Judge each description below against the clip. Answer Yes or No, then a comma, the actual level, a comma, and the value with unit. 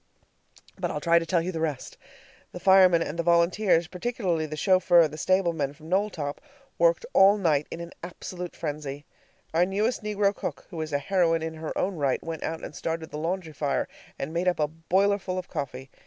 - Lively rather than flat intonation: No, average, 3.1 semitones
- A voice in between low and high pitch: Yes, medium, 170 Hz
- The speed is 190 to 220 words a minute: Yes, average, 200 wpm